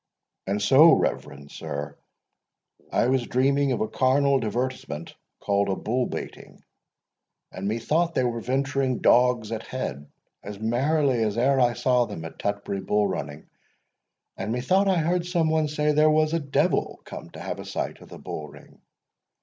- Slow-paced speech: No, average, 165 wpm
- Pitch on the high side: No, low, 125 Hz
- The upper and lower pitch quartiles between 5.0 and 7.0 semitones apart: Yes, average, 5.3 semitones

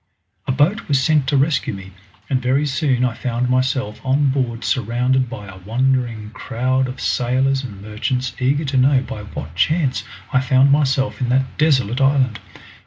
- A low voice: Yes, low, 130 Hz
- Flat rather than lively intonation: Yes, narrow, 2.1 semitones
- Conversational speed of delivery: Yes, average, 175 wpm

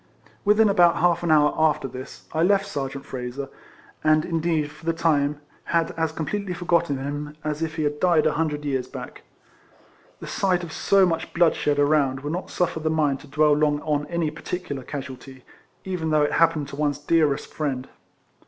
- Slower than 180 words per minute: No, average, 185 wpm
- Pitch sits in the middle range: Yes, medium, 155 Hz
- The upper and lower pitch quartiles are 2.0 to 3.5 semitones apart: Yes, narrow, 2.6 semitones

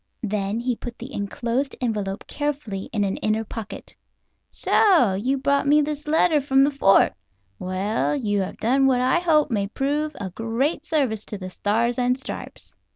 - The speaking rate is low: No, average, 170 wpm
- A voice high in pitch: Yes, high, 245 Hz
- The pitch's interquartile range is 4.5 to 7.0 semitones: Yes, wide, 5.4 semitones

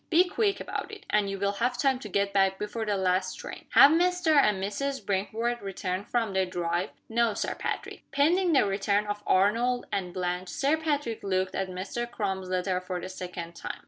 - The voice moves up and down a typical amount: Yes, average, 4.8 semitones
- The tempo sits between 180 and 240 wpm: Yes, average, 200 wpm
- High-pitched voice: Yes, high, 205 Hz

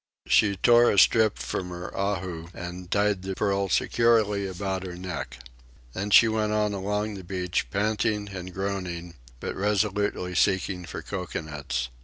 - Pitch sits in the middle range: No, very low, 95 Hz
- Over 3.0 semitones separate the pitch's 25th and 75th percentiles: No, narrow, 2.4 semitones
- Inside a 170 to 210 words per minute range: No, average, 150 wpm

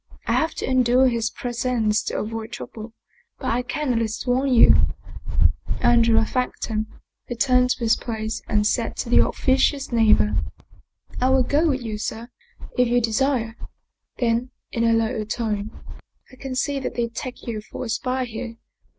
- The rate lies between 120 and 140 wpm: No, average, 175 wpm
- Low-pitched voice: No, high, 235 Hz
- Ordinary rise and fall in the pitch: No, narrow, 2.3 semitones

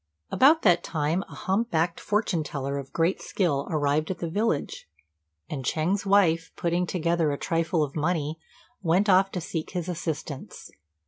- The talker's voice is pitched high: No, medium, 165 Hz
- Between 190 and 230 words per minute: No, average, 165 wpm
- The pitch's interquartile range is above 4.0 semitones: No, average, 3.3 semitones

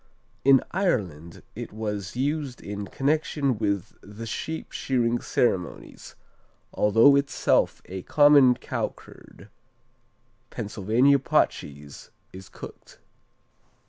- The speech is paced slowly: Yes, slow, 100 wpm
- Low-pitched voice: Yes, low, 115 Hz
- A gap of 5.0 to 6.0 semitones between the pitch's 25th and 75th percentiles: Yes, wide, 5.6 semitones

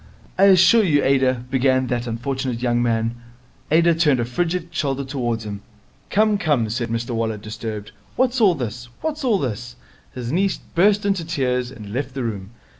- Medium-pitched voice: No, low, 130 Hz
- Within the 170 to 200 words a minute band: Yes, average, 180 wpm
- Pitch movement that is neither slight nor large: No, wide, 6.3 semitones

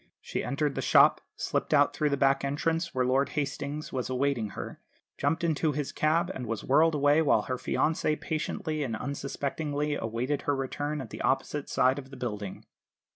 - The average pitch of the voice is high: No, medium, 140 Hz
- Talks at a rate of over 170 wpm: Yes, average, 180 wpm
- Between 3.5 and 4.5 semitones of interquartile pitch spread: No, narrow, 2.5 semitones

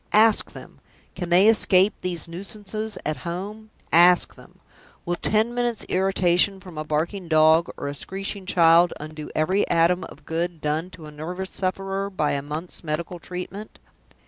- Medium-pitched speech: Yes, medium, 180 Hz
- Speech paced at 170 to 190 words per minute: No, average, 160 wpm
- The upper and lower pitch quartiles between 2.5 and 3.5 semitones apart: Yes, average, 3.1 semitones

